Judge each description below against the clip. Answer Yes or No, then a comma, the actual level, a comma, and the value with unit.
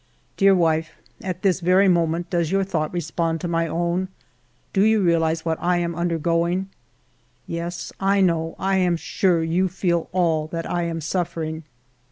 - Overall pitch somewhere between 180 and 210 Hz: No, medium, 170 Hz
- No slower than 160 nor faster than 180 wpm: Yes, average, 170 wpm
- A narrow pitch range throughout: Yes, narrow, 1.9 semitones